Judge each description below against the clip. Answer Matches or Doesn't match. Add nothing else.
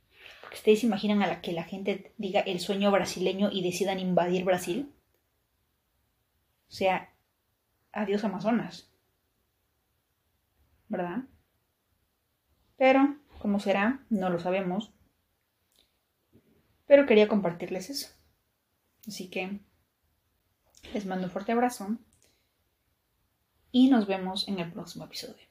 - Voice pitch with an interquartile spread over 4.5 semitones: Doesn't match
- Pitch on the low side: Doesn't match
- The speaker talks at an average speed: Doesn't match